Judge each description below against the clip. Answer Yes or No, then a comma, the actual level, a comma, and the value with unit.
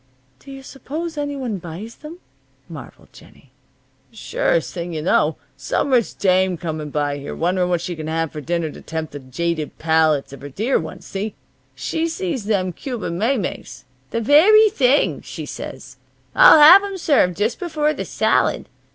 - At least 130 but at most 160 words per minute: No, average, 170 wpm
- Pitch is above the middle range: Yes, high, 200 Hz